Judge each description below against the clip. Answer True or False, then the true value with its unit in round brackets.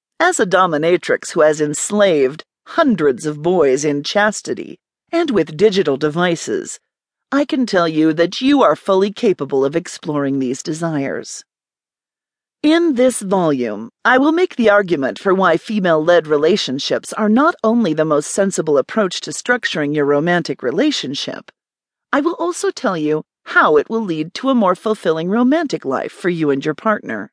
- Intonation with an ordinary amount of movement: False (7.9 semitones)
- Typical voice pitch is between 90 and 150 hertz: False (190 Hz)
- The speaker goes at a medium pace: True (160 wpm)